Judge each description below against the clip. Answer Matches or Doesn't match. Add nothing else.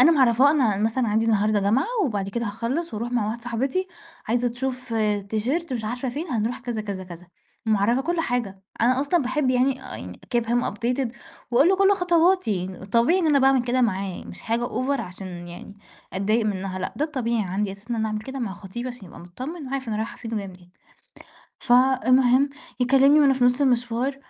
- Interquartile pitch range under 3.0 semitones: Doesn't match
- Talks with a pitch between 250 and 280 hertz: Doesn't match